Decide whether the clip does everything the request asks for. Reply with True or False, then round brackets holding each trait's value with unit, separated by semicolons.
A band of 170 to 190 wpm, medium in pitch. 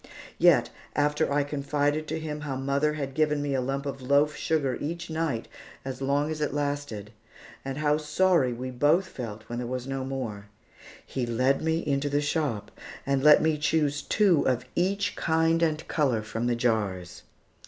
True (180 wpm; 145 Hz)